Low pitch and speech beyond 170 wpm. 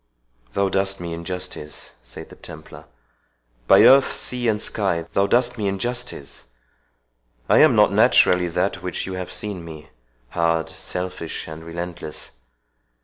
No: very low, 90 Hz; average, 140 wpm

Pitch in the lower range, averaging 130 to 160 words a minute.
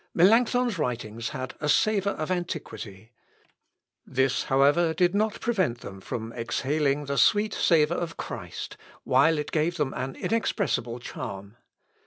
No: medium, 150 Hz; average, 140 wpm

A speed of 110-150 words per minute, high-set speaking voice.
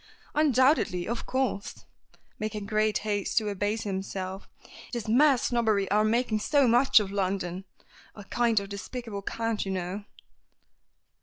Yes: average, 140 wpm; high, 215 Hz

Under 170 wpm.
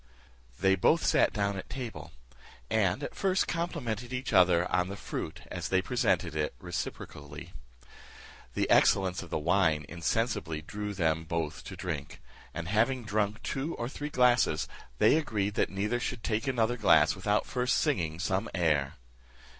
Yes: average, 155 wpm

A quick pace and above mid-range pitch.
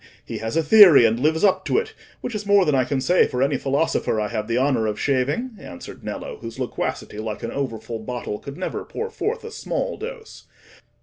No: fast, 225 wpm; medium, 140 Hz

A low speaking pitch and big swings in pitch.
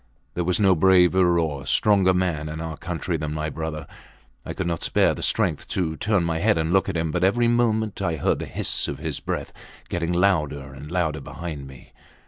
No: very low, 85 Hz; average, 3.3 semitones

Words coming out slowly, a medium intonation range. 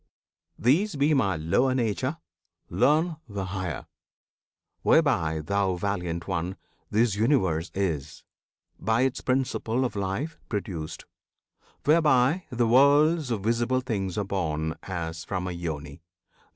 No: slow, 120 wpm; wide, 6.8 semitones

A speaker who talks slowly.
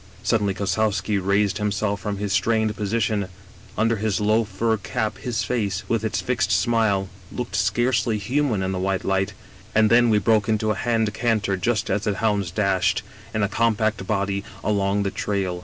No: average, 180 wpm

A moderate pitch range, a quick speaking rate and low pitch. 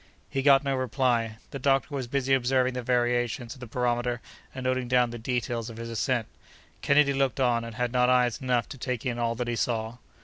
No: narrow, 1.7 semitones; fast, 215 wpm; low, 125 Hz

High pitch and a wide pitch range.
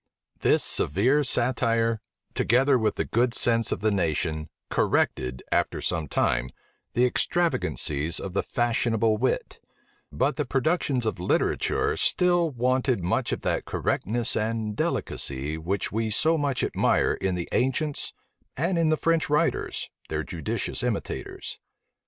No: low, 115 Hz; wide, 6.1 semitones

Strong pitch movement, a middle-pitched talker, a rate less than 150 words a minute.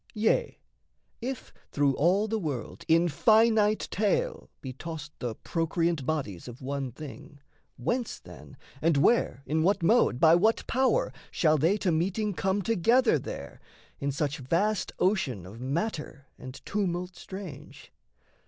Yes: wide, 6.8 semitones; medium, 170 Hz; average, 140 wpm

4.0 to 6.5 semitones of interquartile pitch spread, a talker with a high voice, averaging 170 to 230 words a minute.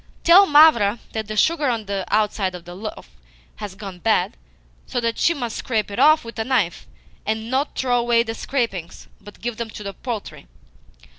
No: average, 3.5 semitones; high, 225 Hz; average, 195 wpm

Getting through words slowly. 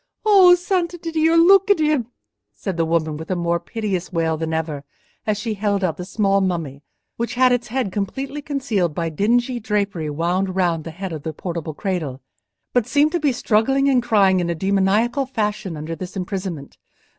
No: average, 185 wpm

